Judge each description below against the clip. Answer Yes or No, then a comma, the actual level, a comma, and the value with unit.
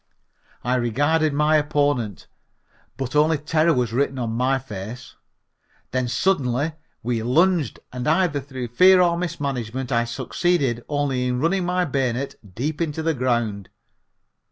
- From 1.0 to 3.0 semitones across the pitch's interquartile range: No, average, 4.2 semitones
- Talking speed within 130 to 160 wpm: Yes, slow, 135 wpm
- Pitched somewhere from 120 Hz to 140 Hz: Yes, low, 135 Hz